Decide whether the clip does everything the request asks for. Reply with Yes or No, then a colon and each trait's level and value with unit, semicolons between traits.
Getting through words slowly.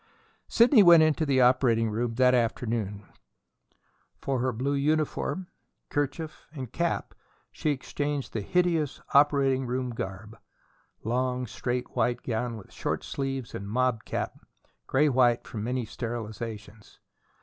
Yes: slow, 125 wpm